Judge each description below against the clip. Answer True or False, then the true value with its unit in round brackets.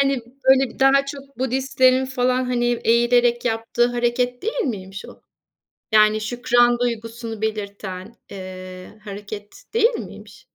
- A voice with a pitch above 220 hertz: True (240 Hz)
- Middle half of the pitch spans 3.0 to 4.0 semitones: True (3.3 semitones)